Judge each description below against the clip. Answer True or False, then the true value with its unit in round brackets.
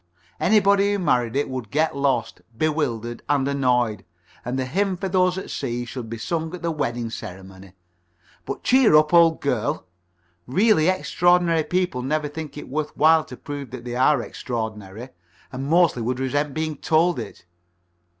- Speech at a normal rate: True (165 wpm)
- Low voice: False (145 Hz)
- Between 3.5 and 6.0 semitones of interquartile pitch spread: True (5.2 semitones)